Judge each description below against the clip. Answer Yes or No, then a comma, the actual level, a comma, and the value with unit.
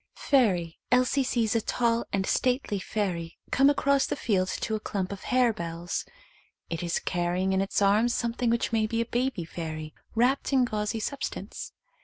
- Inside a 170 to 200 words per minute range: Yes, average, 175 wpm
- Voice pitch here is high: Yes, high, 215 Hz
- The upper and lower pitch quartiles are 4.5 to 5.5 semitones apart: Yes, average, 5.0 semitones